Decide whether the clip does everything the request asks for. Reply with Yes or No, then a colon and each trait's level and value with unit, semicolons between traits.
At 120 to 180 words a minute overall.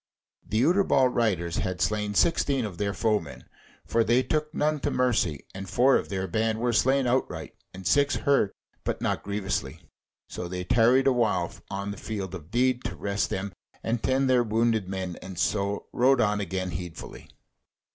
Yes: average, 175 wpm